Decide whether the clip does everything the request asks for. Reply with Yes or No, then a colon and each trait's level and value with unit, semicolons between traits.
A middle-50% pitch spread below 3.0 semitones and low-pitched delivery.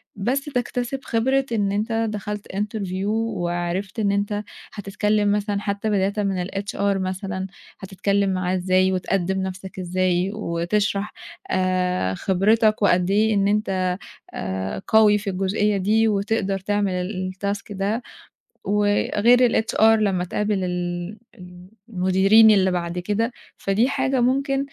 No: narrow, 2.4 semitones; high, 200 Hz